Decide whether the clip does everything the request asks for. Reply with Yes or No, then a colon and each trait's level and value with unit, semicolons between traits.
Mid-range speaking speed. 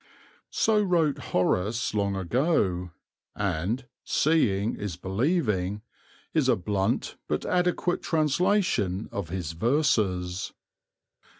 No: slow, 90 wpm